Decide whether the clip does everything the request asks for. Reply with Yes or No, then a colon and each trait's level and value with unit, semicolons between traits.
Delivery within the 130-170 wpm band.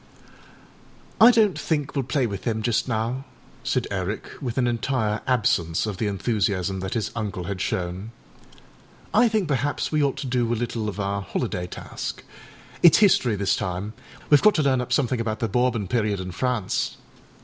No: average, 180 wpm